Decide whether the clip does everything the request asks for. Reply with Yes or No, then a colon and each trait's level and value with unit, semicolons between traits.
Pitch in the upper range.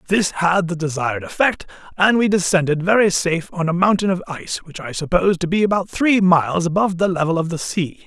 No: medium, 180 Hz